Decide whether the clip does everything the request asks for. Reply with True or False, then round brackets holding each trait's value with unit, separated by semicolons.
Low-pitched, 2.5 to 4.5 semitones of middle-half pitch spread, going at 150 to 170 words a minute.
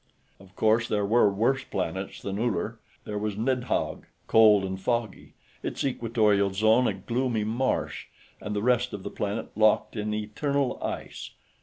True (110 Hz; 2.8 semitones; 155 wpm)